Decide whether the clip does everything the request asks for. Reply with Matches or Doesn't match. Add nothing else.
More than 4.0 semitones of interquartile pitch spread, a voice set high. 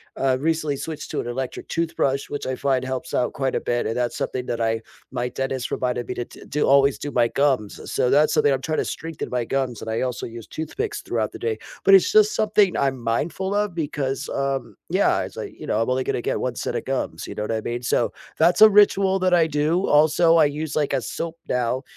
Doesn't match